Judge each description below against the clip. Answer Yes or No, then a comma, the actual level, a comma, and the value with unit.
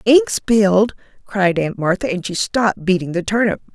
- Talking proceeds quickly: No, average, 175 wpm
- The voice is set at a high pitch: Yes, high, 200 Hz